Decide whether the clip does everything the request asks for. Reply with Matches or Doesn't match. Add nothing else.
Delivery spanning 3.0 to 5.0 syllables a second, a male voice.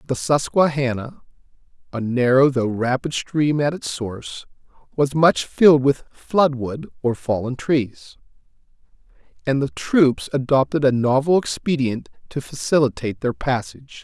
Matches